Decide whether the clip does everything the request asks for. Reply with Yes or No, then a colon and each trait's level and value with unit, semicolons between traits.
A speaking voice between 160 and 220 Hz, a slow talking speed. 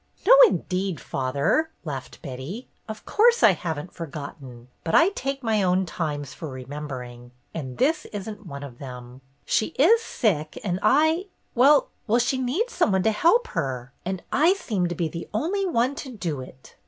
No: medium, 185 Hz; average, 185 wpm